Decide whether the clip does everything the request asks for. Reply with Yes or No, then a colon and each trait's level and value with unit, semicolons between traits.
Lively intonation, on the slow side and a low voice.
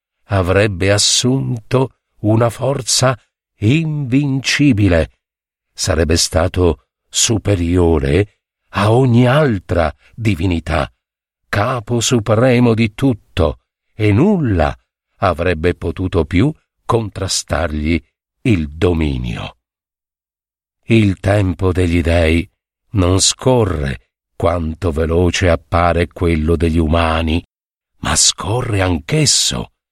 Yes: wide, 5.7 semitones; slow, 80 wpm; very low, 95 Hz